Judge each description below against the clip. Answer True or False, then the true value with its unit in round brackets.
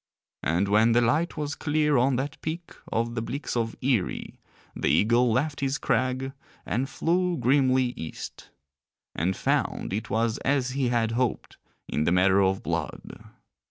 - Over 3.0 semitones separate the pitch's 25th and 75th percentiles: True (3.9 semitones)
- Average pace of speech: True (160 wpm)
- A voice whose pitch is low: True (125 Hz)